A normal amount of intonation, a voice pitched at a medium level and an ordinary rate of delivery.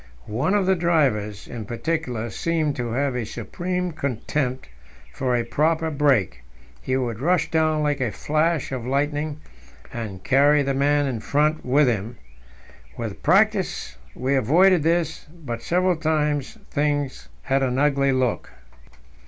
Yes: average, 4.3 semitones; medium, 145 Hz; average, 145 wpm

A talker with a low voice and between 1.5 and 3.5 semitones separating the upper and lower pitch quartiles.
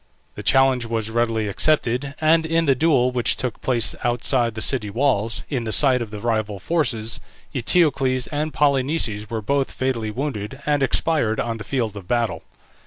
No: low, 125 Hz; average, 3.9 semitones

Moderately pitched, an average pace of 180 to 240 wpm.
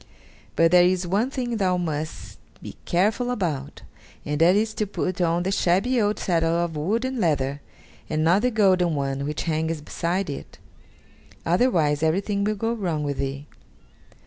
No: medium, 175 Hz; average, 170 wpm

